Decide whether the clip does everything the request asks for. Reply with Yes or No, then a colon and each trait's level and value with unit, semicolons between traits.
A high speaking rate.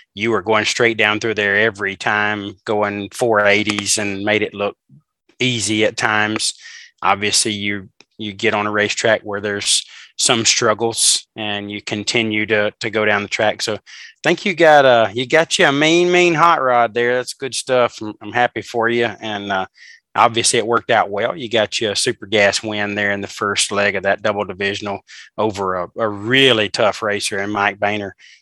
No: average, 195 wpm